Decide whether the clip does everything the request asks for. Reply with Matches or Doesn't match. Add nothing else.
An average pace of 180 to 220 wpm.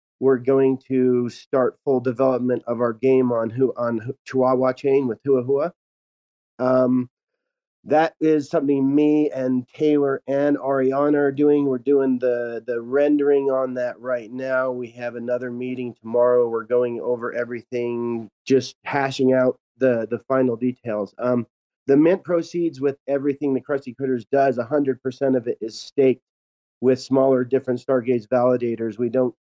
Doesn't match